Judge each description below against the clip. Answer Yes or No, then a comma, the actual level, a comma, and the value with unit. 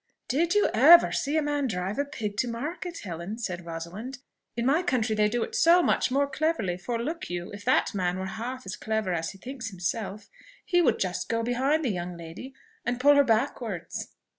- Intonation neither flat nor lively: No, wide, 7.0 semitones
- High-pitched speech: Yes, high, 230 Hz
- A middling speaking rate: No, fast, 210 wpm